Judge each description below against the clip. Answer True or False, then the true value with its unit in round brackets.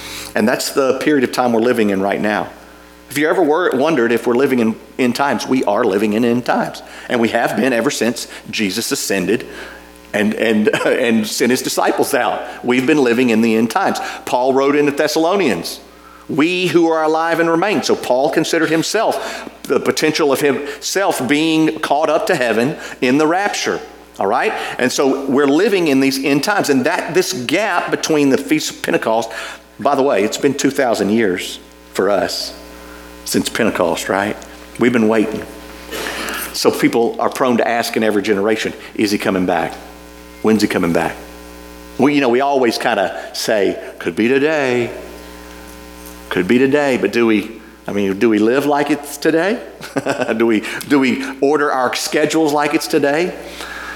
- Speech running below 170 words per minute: False (180 wpm)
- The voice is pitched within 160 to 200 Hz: False (115 Hz)